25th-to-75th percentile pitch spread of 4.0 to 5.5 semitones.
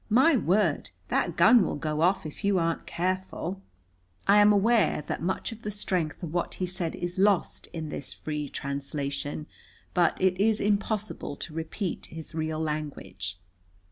Yes: average, 4.5 semitones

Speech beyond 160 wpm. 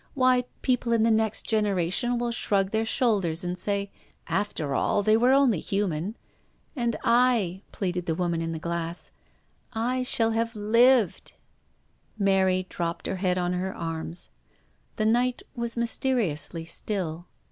No: average, 155 wpm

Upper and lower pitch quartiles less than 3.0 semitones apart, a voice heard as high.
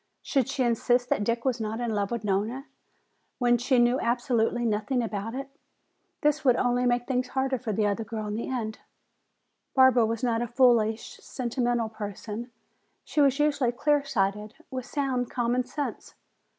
Yes: narrow, 2.6 semitones; high, 240 Hz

